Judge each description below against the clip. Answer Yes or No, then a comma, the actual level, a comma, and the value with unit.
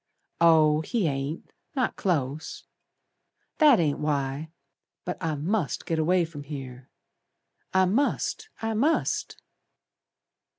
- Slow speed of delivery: Yes, slow, 110 wpm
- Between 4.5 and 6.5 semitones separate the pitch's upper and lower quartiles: Yes, average, 5.0 semitones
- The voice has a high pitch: No, medium, 160 Hz